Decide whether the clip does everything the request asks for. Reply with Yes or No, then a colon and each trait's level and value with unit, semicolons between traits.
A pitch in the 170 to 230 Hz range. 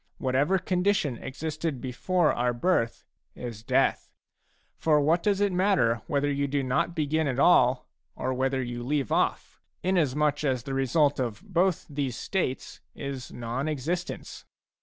No: medium, 140 Hz